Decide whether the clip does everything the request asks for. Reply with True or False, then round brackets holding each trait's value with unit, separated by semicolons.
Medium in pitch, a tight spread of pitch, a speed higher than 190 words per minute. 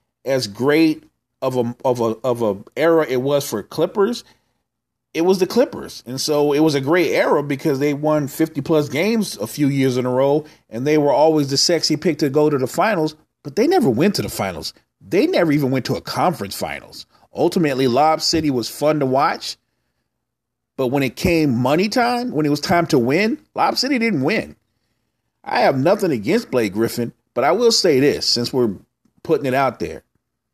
False (145 Hz; 3.9 semitones; 200 wpm)